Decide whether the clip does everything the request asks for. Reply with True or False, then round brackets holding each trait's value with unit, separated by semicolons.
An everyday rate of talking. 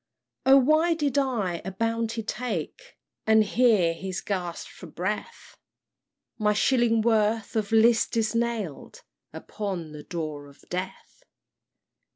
False (120 wpm)